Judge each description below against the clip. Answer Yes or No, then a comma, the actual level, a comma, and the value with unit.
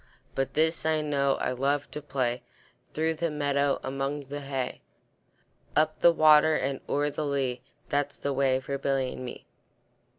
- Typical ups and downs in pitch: No, narrow, 1.9 semitones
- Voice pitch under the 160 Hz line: Yes, medium, 140 Hz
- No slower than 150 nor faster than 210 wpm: Yes, average, 165 wpm